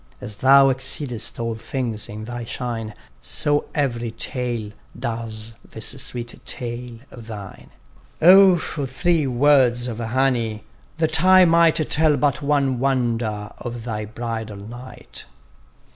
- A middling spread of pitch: Yes, average, 3.5 semitones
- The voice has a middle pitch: No, low, 120 Hz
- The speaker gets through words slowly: Yes, slow, 130 wpm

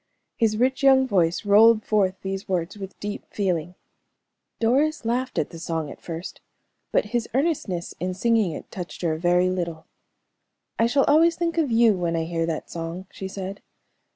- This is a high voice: Yes, high, 195 Hz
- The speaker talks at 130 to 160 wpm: No, average, 180 wpm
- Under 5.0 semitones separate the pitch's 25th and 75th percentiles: No, average, 5.3 semitones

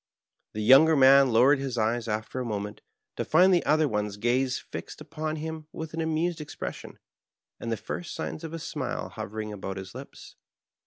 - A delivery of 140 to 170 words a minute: No, average, 180 wpm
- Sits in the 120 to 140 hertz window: Yes, low, 135 Hz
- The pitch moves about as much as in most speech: No, wide, 6.3 semitones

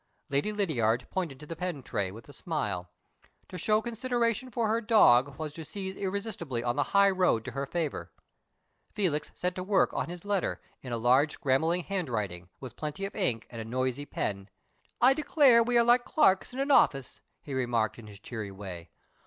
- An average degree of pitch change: No, wide, 8.9 semitones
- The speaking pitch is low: No, medium, 155 Hz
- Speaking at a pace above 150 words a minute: Yes, average, 195 wpm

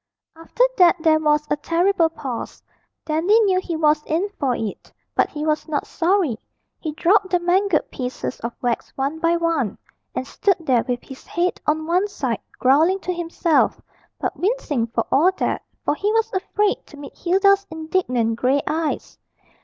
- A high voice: Yes, very high, 320 Hz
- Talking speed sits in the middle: Yes, average, 170 wpm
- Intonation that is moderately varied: Yes, average, 4.7 semitones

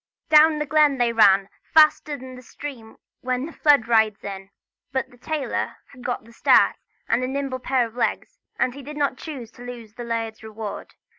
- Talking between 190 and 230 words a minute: Yes, average, 200 wpm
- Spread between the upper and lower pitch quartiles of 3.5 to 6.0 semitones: Yes, average, 3.9 semitones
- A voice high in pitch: Yes, very high, 250 Hz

